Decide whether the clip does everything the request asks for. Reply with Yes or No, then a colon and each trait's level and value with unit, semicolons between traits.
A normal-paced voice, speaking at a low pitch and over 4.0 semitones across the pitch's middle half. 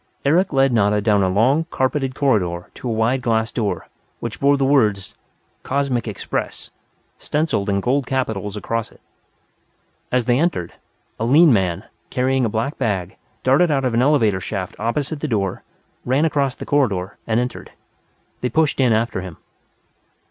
Yes: average, 165 wpm; low, 120 Hz; average, 4.8 semitones